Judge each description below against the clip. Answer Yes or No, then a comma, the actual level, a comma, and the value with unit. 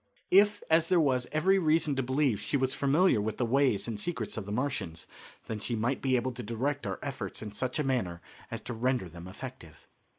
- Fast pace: Yes, fast, 220 wpm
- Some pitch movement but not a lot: Yes, average, 4.7 semitones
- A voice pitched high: No, low, 130 Hz